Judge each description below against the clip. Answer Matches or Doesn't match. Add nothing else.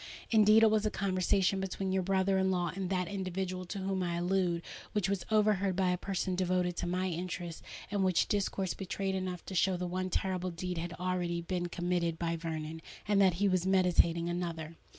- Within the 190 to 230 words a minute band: Matches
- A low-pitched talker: Doesn't match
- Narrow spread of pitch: Matches